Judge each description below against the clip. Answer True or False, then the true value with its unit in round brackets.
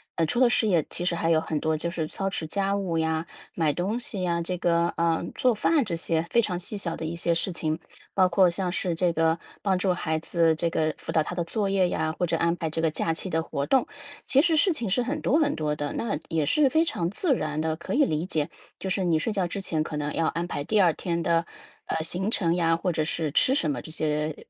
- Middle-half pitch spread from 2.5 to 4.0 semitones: True (3.5 semitones)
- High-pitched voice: False (170 Hz)